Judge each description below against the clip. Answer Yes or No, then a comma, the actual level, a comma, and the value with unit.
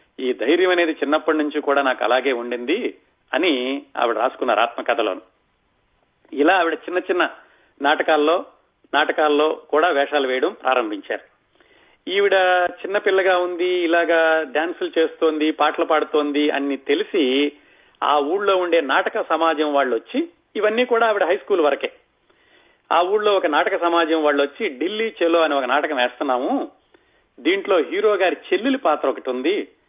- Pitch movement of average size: No, wide, 5.8 semitones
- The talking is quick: Yes, fast, 135 wpm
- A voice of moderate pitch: Yes, medium, 170 Hz